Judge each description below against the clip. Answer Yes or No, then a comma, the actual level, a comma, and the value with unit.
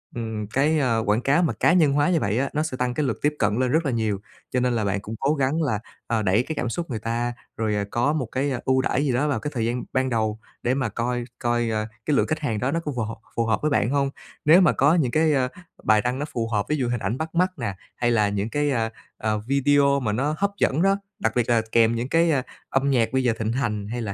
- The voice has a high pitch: No, low, 125 Hz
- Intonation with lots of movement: No, average, 4.3 semitones